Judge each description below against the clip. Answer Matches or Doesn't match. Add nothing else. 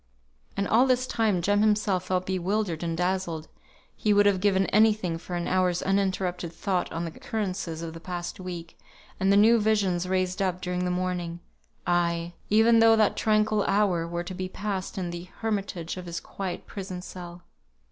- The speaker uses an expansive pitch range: Doesn't match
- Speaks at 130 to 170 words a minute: Doesn't match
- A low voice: Doesn't match